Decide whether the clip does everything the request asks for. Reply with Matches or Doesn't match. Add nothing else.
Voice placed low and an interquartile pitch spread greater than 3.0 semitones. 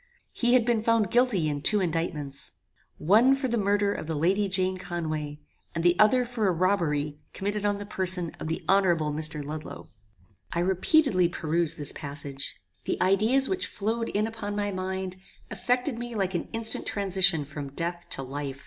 Doesn't match